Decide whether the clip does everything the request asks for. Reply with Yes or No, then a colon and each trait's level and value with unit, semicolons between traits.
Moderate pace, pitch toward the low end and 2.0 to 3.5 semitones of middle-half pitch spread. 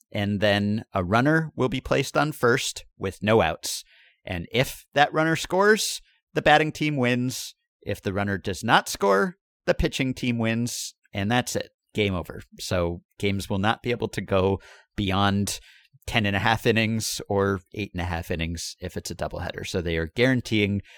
No: average, 185 wpm; low, 110 Hz; average, 4.7 semitones